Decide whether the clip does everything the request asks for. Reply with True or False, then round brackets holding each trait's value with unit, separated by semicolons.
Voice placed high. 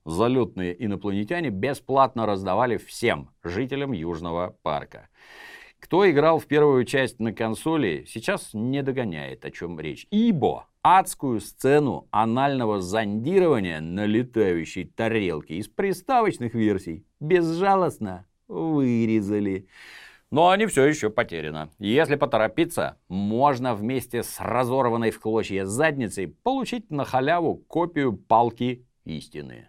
False (115 Hz)